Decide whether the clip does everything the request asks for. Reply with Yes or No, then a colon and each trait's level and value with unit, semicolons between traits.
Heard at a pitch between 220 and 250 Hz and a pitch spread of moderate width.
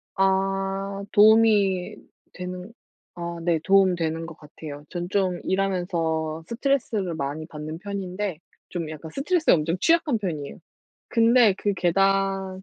No: medium, 185 Hz; average, 3.3 semitones